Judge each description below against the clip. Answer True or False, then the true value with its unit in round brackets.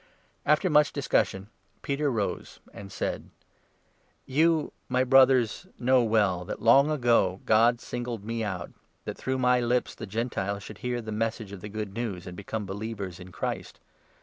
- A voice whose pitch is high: False (115 Hz)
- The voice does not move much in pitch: False (3.9 semitones)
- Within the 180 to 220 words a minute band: False (170 wpm)